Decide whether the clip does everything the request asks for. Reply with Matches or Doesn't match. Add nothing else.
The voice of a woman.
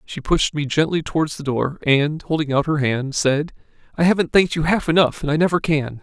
Doesn't match